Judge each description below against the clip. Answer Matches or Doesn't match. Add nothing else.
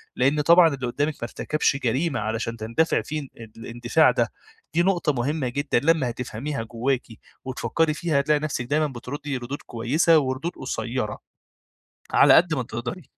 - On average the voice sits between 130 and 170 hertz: Matches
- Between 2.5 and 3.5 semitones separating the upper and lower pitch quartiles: Doesn't match